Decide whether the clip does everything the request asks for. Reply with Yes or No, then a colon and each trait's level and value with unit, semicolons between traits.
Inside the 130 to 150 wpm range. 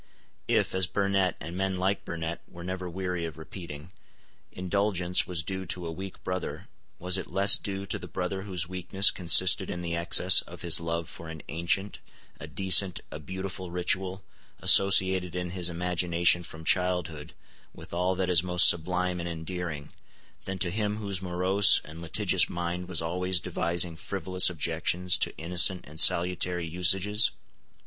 No: average, 160 wpm